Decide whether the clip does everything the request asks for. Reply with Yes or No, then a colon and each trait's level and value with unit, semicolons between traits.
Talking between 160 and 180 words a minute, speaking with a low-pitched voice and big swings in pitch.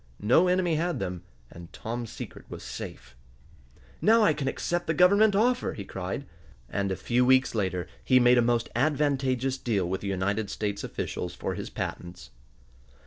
Yes: average, 170 wpm; low, 125 Hz; wide, 8.1 semitones